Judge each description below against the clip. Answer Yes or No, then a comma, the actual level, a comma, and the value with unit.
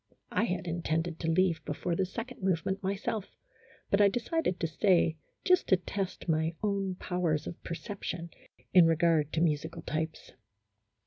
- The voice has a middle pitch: Yes, medium, 175 Hz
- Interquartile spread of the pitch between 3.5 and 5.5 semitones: No, average, 3.0 semitones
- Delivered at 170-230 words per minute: No, average, 155 wpm